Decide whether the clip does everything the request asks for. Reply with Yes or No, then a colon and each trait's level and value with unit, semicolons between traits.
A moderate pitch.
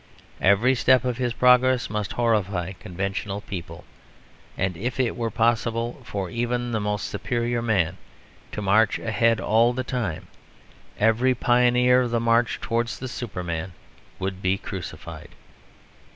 No: low, 115 Hz